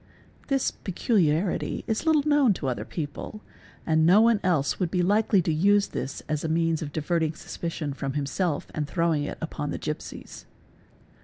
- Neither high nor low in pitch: Yes, medium, 165 Hz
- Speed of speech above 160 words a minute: Yes, average, 170 wpm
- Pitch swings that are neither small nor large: Yes, average, 4.9 semitones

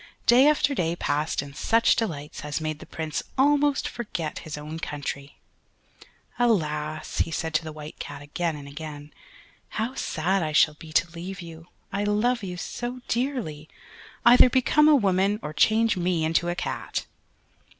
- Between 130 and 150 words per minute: No, average, 165 wpm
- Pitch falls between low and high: Yes, medium, 170 Hz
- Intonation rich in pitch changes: Yes, wide, 6.9 semitones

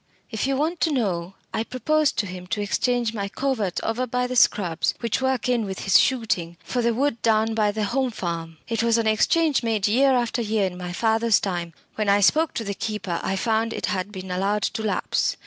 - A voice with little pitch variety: No, average, 4.0 semitones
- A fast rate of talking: Yes, fast, 220 wpm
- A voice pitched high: Yes, high, 220 Hz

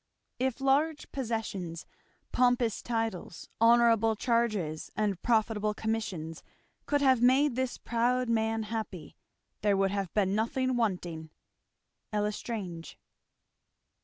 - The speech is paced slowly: Yes, slow, 105 wpm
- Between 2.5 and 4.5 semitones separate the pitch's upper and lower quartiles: Yes, average, 3.6 semitones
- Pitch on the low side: No, high, 225 Hz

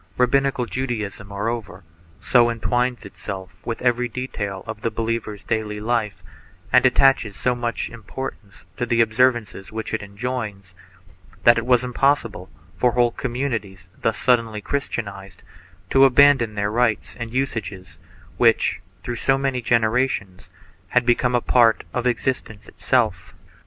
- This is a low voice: Yes, low, 115 Hz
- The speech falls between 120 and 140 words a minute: Yes, slow, 135 wpm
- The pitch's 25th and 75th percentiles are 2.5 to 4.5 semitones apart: Yes, average, 3.0 semitones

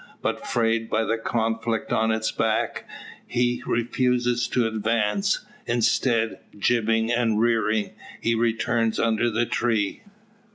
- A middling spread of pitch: No, narrow, 1.2 semitones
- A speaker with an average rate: No, slow, 120 wpm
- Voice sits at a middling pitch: No, low, 115 Hz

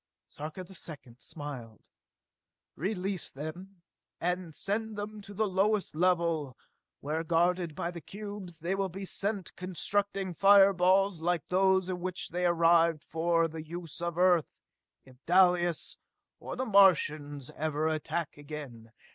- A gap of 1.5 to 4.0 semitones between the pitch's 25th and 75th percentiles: Yes, average, 3.4 semitones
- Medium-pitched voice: Yes, medium, 175 Hz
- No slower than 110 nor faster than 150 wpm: Yes, average, 140 wpm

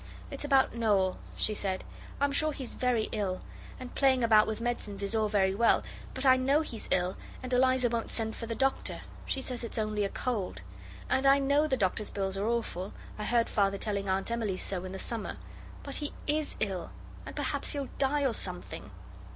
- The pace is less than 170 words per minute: No, average, 200 wpm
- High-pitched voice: Yes, high, 230 Hz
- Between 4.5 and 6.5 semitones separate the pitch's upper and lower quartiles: Yes, average, 4.8 semitones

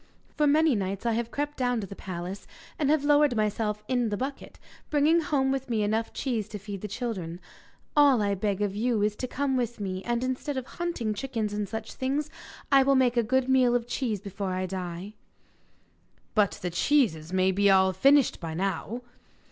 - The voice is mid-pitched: No, high, 230 Hz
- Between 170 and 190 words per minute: No, average, 200 wpm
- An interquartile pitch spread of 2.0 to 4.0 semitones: No, average, 5.0 semitones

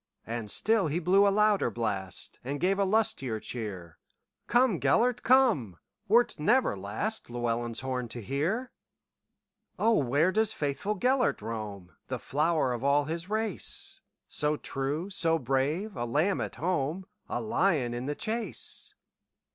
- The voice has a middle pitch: Yes, medium, 155 Hz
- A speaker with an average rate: No, slow, 120 wpm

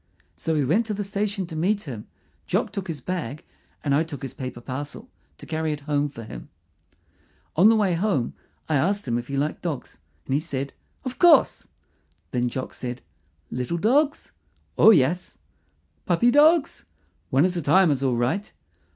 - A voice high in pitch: No, medium, 160 Hz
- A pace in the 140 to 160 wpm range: No, average, 180 wpm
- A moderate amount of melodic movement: No, wide, 6.7 semitones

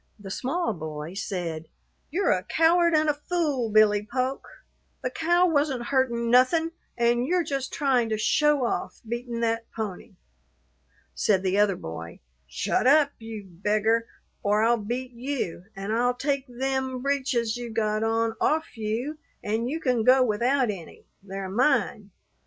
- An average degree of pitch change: Yes, average, 4.4 semitones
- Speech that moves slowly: No, average, 150 wpm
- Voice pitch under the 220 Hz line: No, high, 235 Hz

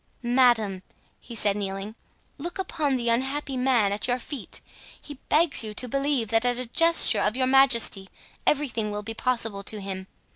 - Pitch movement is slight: No, average, 4.2 semitones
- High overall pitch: Yes, high, 240 Hz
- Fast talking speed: No, average, 175 wpm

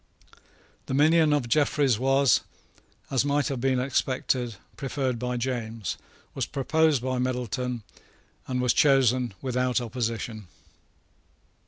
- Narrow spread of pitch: Yes, narrow, 2.0 semitones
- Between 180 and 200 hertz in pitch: No, low, 130 Hz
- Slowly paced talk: Yes, slow, 115 wpm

